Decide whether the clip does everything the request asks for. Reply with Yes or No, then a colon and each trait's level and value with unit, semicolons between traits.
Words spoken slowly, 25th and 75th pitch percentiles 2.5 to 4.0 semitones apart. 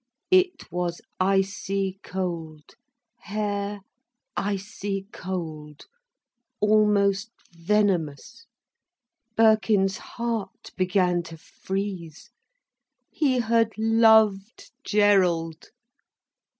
Yes: slow, 65 wpm; average, 3.1 semitones